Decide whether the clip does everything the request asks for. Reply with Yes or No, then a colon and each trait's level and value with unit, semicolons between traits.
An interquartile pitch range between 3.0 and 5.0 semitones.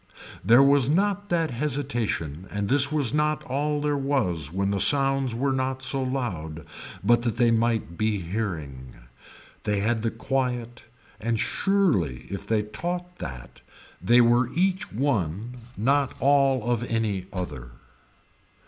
No: wide, 5.6 semitones